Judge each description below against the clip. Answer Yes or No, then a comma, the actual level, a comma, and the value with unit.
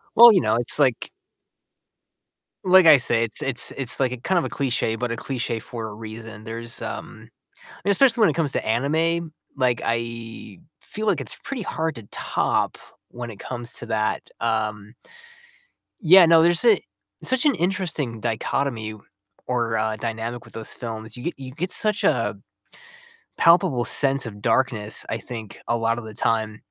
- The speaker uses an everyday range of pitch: No, wide, 6.2 semitones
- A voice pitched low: Yes, low, 120 Hz